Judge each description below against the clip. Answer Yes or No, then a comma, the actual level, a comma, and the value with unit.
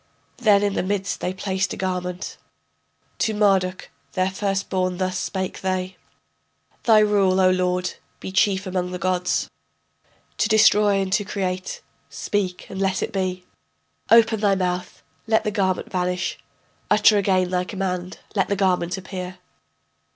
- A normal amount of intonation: No, narrow, 1.6 semitones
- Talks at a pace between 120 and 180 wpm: Yes, average, 150 wpm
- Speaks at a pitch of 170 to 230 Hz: Yes, high, 190 Hz